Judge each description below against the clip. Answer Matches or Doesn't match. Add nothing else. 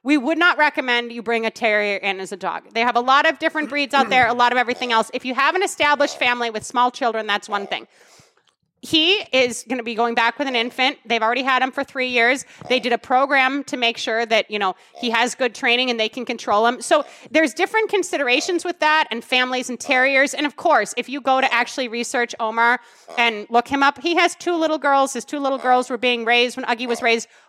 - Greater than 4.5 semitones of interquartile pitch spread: Doesn't match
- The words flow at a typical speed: Doesn't match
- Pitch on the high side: Matches